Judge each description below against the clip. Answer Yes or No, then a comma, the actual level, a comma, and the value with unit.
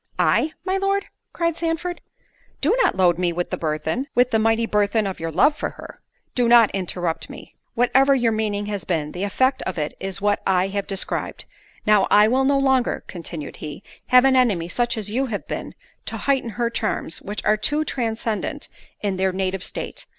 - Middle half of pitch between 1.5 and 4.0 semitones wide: No, wide, 5.4 semitones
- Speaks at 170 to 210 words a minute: Yes, average, 195 wpm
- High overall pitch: Yes, high, 215 Hz